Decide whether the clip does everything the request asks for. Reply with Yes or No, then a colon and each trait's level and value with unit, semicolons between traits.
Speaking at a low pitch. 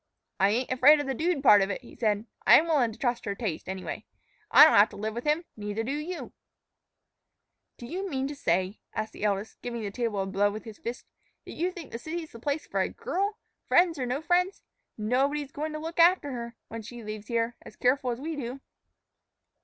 No: high, 245 Hz